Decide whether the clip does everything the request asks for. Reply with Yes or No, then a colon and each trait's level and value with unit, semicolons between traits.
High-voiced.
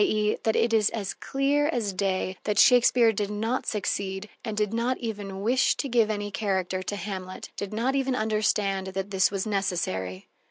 Yes: high, 210 Hz